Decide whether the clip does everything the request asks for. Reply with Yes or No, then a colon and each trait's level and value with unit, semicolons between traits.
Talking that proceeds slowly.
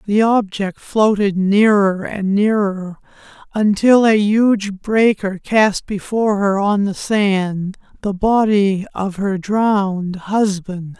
Yes: slow, 120 wpm